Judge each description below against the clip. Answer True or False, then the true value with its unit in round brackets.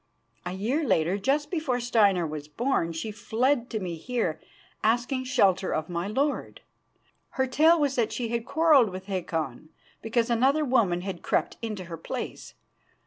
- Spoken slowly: False (160 wpm)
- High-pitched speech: True (225 Hz)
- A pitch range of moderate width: False (6.2 semitones)